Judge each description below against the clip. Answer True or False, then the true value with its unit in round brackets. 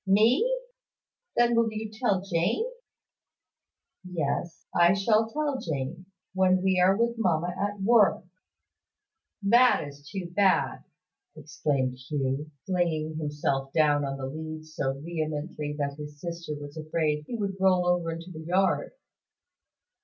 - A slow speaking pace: True (130 wpm)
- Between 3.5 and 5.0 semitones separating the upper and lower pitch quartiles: True (4.7 semitones)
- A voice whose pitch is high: False (170 Hz)